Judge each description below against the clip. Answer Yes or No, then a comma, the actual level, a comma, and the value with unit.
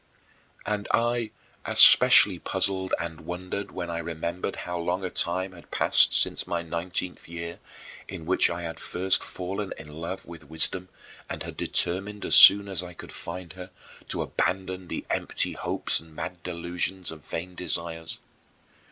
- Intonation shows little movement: Yes, narrow, 1.8 semitones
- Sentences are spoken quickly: No, average, 160 wpm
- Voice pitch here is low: Yes, very low, 90 Hz